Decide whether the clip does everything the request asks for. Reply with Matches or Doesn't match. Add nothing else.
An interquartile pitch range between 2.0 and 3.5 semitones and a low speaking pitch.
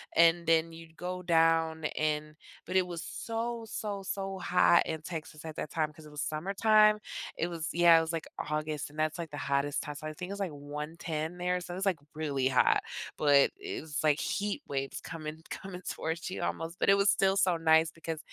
Doesn't match